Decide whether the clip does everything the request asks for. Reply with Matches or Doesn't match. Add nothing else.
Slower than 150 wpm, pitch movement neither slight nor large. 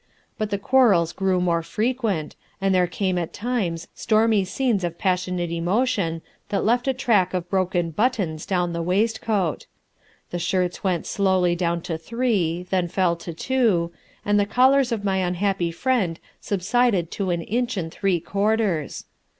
Doesn't match